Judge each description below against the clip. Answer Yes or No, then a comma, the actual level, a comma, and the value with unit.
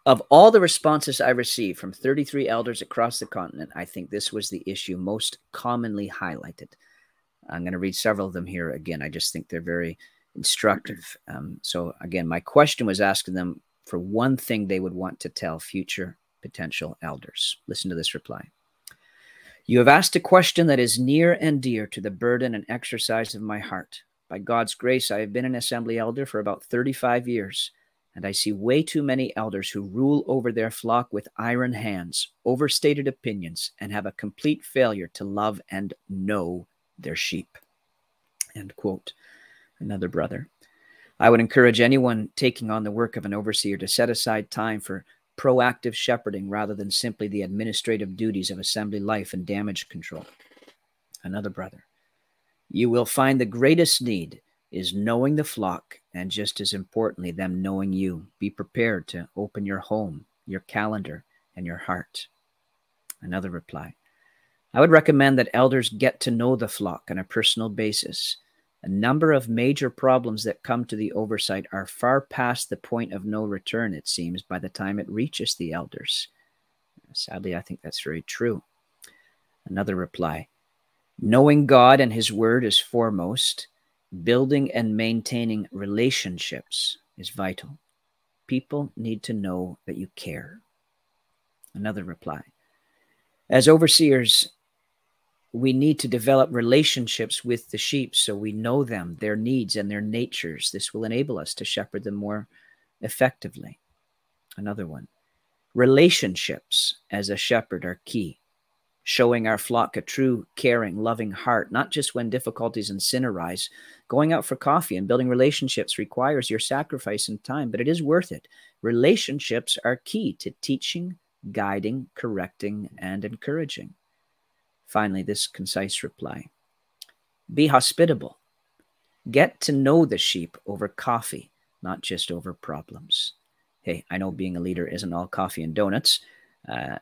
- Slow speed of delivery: No, average, 160 wpm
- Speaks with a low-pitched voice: Yes, low, 110 Hz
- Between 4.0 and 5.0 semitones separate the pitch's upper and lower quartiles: Yes, average, 4.6 semitones